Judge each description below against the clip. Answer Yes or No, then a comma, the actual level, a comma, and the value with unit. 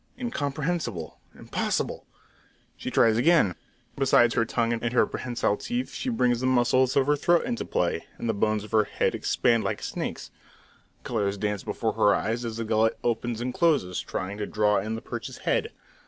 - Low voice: Yes, low, 115 Hz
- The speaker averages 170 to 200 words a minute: Yes, average, 185 wpm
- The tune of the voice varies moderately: Yes, average, 3.7 semitones